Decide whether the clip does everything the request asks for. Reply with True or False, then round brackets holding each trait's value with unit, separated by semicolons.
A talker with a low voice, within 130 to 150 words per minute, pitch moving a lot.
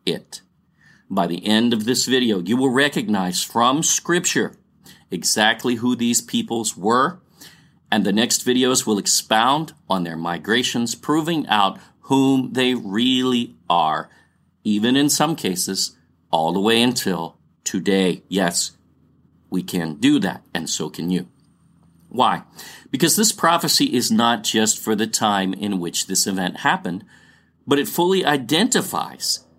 True (115 Hz; 140 wpm; 5.9 semitones)